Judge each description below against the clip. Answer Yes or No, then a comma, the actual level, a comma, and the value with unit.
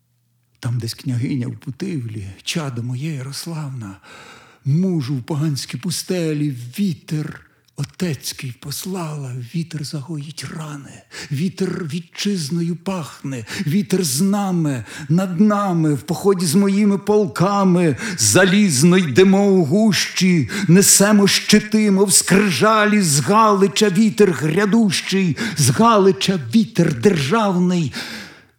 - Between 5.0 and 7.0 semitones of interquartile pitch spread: Yes, wide, 5.6 semitones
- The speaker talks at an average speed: No, slow, 95 wpm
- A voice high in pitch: No, medium, 175 Hz